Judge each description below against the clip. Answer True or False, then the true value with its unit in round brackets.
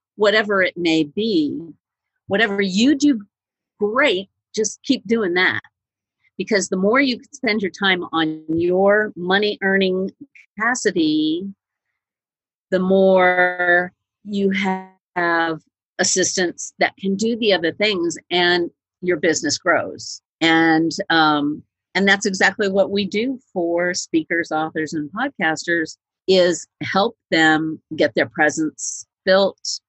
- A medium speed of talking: False (115 wpm)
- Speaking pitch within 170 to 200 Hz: True (190 Hz)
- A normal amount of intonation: True (3.9 semitones)